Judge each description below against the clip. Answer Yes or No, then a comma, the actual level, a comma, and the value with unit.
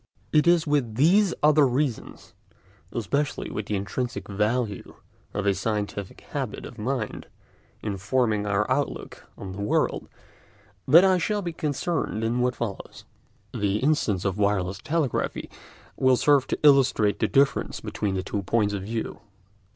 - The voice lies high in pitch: No, low, 115 Hz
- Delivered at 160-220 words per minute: No, average, 150 wpm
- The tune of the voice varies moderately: No, wide, 5.8 semitones